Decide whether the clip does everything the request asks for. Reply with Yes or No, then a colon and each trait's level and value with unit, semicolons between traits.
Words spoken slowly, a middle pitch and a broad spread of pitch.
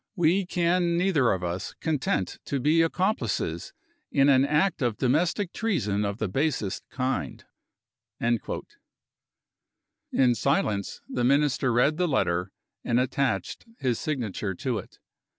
No: slow, 125 wpm; low, 130 Hz; wide, 7.0 semitones